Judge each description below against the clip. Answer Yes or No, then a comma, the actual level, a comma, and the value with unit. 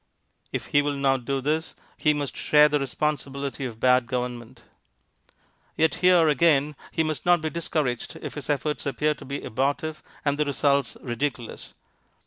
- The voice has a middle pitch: Yes, medium, 145 Hz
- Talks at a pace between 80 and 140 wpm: No, average, 160 wpm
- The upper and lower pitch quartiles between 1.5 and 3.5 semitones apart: Yes, narrow, 2.4 semitones